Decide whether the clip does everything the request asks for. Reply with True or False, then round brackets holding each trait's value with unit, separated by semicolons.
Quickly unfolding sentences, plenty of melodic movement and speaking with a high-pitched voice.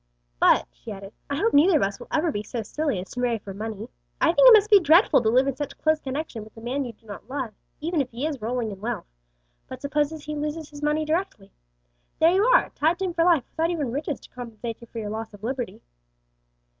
True (250 wpm; 5.9 semitones; 275 Hz)